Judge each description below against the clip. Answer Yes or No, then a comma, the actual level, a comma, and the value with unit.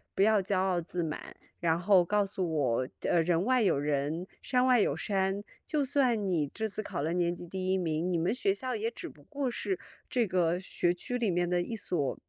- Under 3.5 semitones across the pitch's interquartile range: No, average, 4.3 semitones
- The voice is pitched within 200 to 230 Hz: No, medium, 185 Hz